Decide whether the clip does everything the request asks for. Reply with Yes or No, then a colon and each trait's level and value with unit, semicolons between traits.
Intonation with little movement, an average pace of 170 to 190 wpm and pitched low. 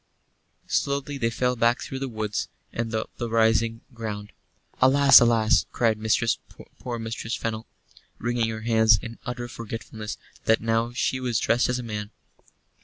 No: narrow, 1.6 semitones; average, 150 wpm; low, 115 Hz